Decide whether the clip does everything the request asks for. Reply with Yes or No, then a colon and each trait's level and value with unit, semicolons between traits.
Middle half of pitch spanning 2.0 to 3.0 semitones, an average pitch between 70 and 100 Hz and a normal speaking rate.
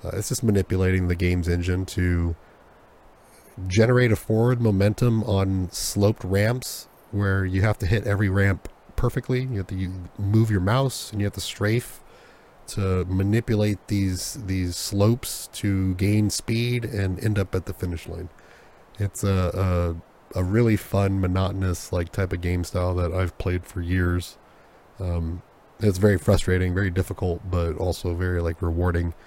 Yes: narrow, 2.6 semitones; very low, 95 Hz; average, 160 wpm